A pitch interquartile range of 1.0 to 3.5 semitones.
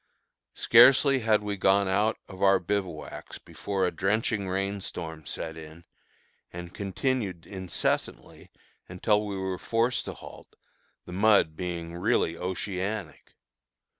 Yes: average, 2.9 semitones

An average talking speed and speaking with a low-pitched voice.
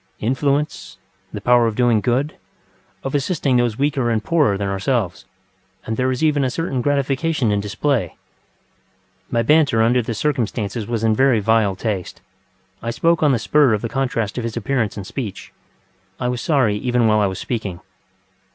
Yes: average, 180 wpm; low, 120 Hz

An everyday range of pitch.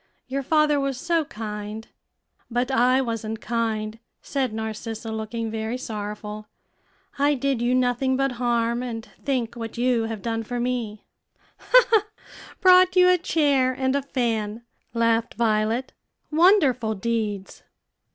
Yes: average, 3.1 semitones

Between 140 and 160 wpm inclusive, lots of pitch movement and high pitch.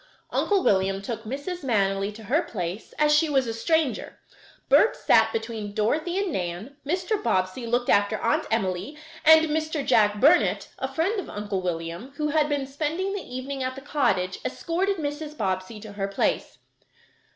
No: average, 170 wpm; wide, 7.5 semitones; very high, 260 Hz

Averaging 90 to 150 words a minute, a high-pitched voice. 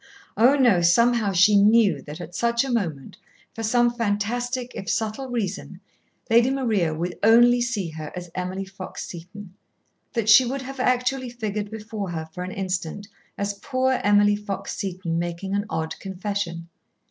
No: average, 160 wpm; high, 205 Hz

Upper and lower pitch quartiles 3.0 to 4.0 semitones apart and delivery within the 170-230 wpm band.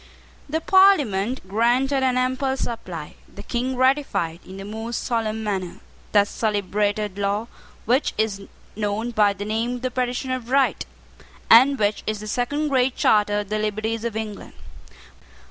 No: average, 3.7 semitones; average, 155 wpm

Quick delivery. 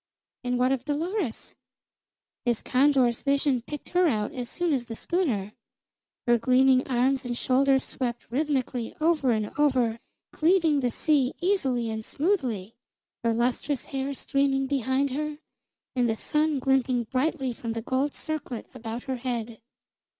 No: average, 145 wpm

